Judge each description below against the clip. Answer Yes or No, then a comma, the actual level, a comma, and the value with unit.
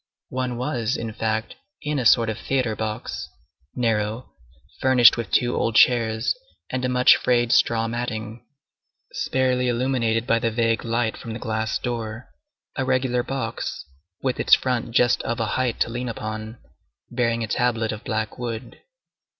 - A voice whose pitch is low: Yes, low, 115 Hz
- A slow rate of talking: No, average, 160 wpm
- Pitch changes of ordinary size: No, narrow, 2.1 semitones